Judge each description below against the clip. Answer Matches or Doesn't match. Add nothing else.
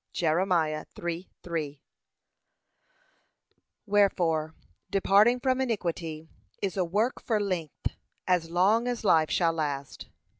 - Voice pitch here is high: Doesn't match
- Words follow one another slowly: Matches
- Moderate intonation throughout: Matches